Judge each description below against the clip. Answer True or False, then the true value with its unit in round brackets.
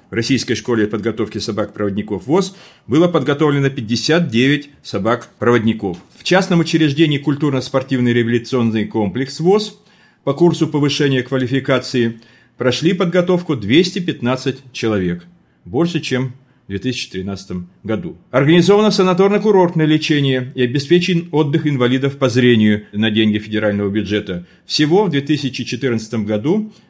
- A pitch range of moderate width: False (6.1 semitones)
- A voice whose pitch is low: True (130 Hz)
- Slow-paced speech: True (105 wpm)